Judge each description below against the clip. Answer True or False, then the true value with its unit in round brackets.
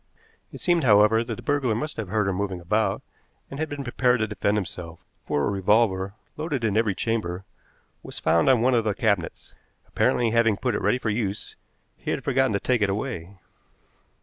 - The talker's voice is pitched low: True (110 Hz)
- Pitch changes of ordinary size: True (4.0 semitones)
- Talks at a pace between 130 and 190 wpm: False (200 wpm)